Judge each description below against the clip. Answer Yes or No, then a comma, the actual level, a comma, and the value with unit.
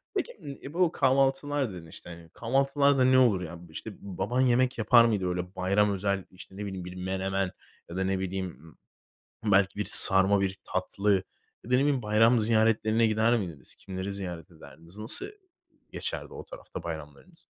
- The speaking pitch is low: Yes, low, 100 Hz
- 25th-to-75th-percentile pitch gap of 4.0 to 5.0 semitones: Yes, average, 4.6 semitones